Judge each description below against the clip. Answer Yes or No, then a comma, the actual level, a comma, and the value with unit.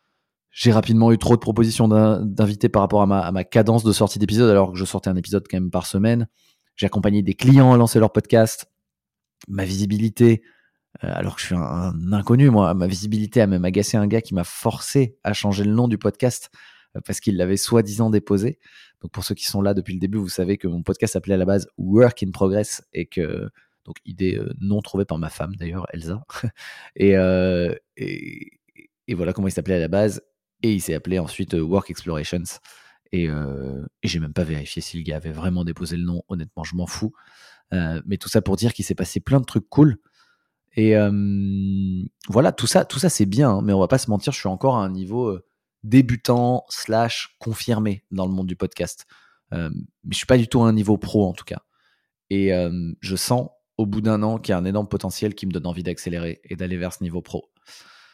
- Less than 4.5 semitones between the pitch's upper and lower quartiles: Yes, average, 3.3 semitones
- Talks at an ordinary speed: No, fast, 225 wpm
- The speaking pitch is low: Yes, low, 100 Hz